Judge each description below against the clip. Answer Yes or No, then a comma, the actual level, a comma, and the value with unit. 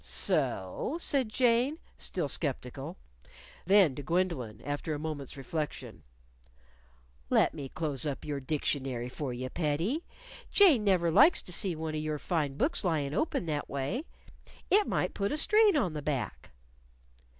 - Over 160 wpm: No, average, 150 wpm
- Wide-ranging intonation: Yes, wide, 7.0 semitones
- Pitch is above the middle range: No, medium, 155 Hz